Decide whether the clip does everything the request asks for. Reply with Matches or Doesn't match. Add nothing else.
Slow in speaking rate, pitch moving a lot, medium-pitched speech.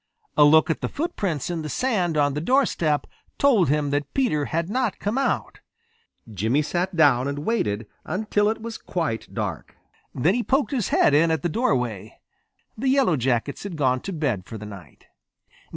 Doesn't match